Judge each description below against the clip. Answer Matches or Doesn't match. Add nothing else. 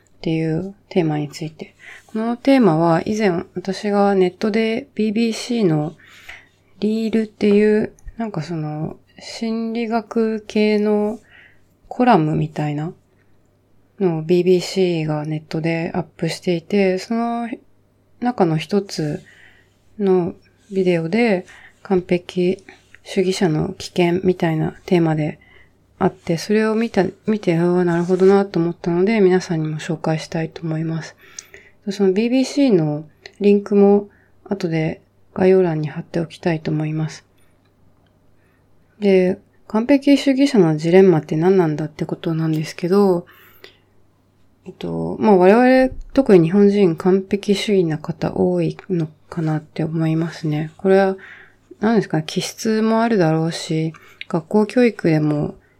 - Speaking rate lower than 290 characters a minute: Matches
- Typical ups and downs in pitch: Matches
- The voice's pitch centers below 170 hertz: Doesn't match